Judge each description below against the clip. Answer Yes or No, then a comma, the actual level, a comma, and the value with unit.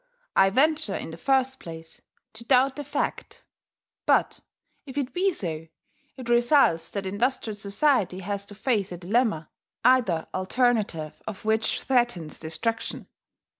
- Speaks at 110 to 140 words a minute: Yes, slow, 135 wpm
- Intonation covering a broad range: Yes, wide, 5.7 semitones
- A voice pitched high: Yes, high, 220 Hz